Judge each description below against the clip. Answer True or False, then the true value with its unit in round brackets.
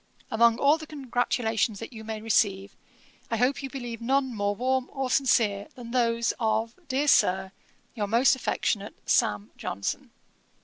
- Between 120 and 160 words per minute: True (150 wpm)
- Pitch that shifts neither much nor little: True (3.3 semitones)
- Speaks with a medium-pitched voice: False (230 Hz)